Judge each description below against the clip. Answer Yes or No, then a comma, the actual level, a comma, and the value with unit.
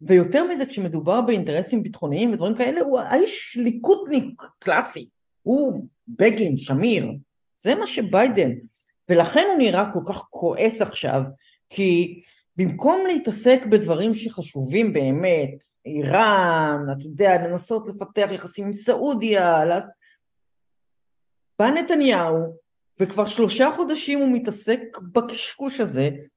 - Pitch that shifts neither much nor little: No, wide, 6.3 semitones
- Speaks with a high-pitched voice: Yes, high, 210 Hz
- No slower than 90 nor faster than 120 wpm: Yes, average, 105 wpm